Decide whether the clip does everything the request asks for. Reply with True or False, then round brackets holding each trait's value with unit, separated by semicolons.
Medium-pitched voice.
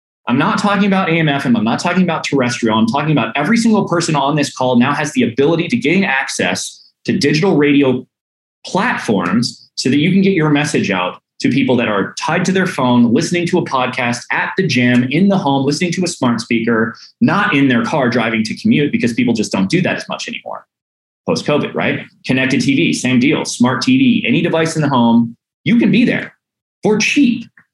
True (150 Hz)